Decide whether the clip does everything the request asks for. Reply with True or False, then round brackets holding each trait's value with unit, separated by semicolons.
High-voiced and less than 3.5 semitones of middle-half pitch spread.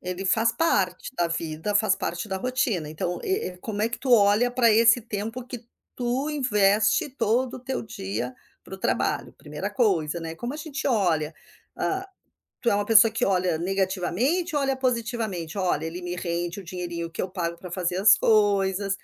False (200 Hz; 5.2 semitones)